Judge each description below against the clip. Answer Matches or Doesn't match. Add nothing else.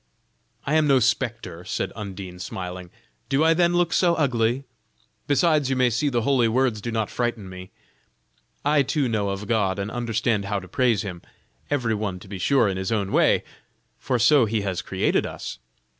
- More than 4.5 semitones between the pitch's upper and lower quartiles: Matches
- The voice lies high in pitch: Doesn't match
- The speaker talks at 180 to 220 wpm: Matches